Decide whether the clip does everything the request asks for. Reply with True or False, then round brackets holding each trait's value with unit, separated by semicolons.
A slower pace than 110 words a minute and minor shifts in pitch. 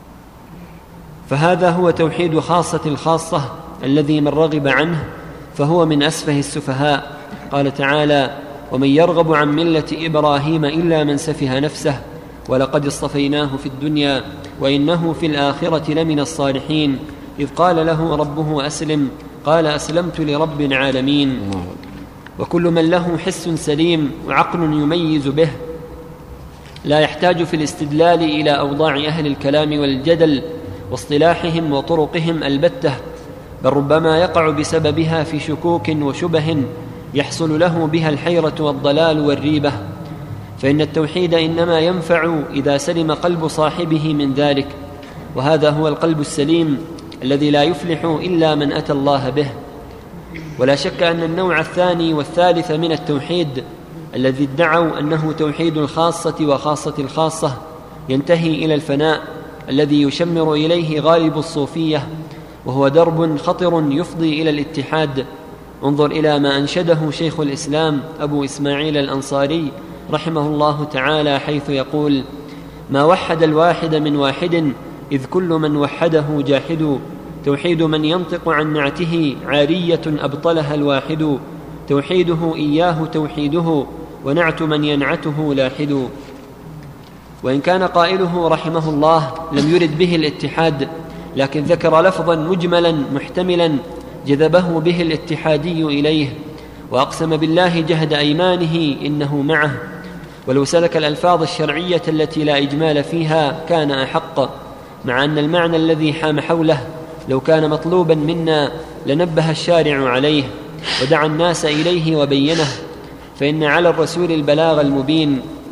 False (115 wpm; 2.2 semitones)